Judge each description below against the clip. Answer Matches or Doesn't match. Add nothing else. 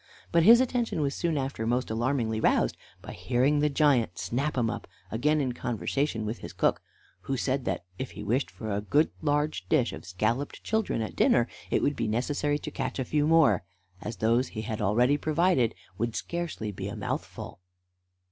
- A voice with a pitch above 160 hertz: Doesn't match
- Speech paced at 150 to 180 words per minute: Doesn't match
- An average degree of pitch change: Matches